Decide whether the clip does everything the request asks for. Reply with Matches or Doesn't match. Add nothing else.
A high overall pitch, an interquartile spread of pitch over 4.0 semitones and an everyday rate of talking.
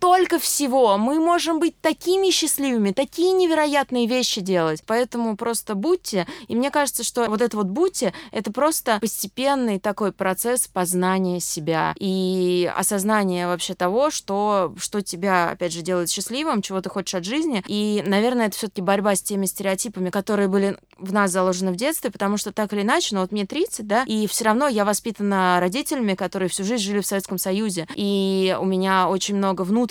Doesn't match